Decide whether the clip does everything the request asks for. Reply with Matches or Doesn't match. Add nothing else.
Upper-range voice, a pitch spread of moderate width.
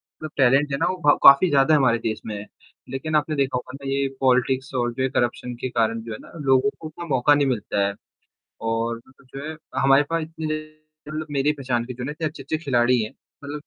Doesn't match